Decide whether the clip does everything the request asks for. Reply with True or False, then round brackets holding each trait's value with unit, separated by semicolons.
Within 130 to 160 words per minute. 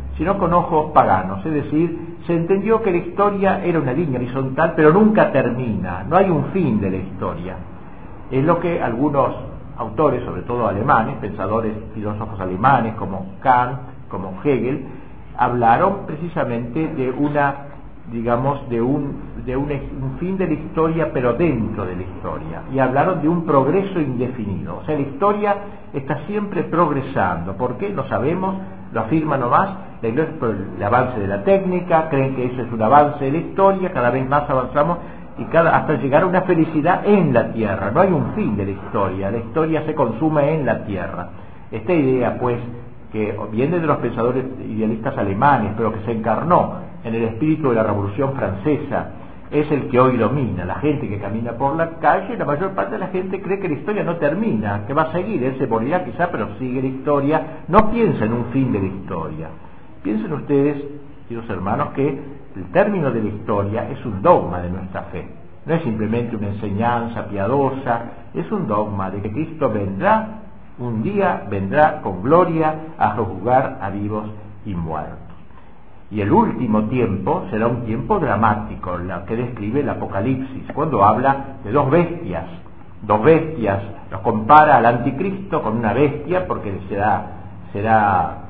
False (175 wpm)